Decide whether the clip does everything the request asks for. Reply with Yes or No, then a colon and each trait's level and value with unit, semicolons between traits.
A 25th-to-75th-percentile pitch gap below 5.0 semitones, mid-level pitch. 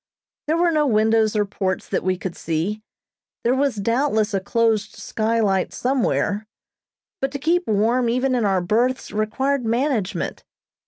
No: average, 4.1 semitones; high, 225 Hz